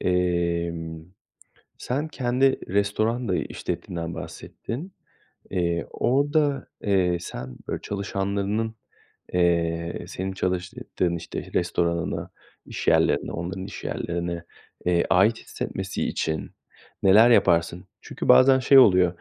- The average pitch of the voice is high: No, very low, 90 Hz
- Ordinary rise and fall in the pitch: Yes, average, 4.8 semitones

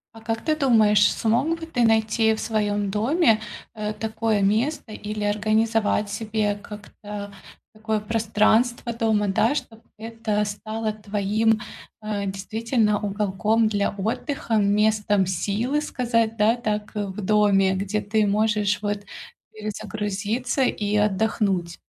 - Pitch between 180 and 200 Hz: No, high, 215 Hz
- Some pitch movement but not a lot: No, narrow, 1.6 semitones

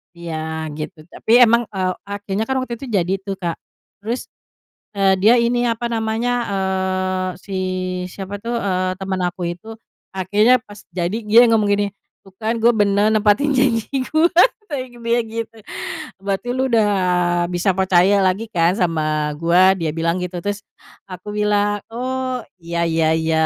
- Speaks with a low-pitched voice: No, high, 200 Hz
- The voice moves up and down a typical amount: Yes, average, 3.9 semitones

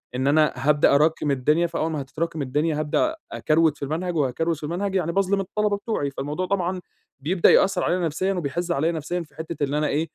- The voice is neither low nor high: Yes, medium, 160 Hz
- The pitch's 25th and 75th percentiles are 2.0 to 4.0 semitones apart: Yes, average, 3.4 semitones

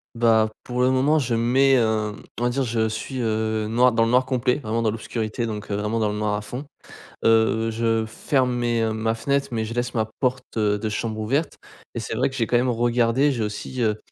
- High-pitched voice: No, low, 115 Hz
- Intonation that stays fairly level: Yes, narrow, 2.2 semitones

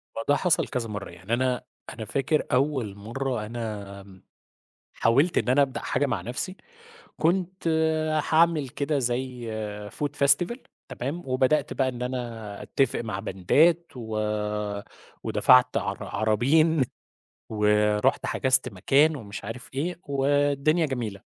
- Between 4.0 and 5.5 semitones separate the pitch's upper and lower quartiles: Yes, average, 4.7 semitones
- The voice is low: Yes, low, 130 Hz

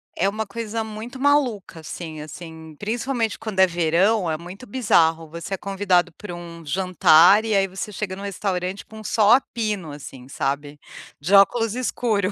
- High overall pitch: Yes, high, 195 Hz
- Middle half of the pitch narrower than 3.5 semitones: No, average, 4.5 semitones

